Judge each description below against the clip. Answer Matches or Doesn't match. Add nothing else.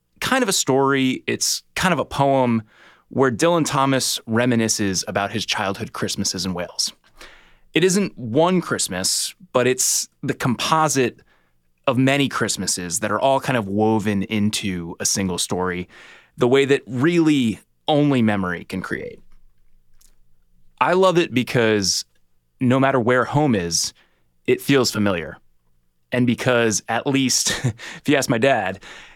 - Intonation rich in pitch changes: Matches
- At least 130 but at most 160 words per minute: Matches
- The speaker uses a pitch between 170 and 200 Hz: Doesn't match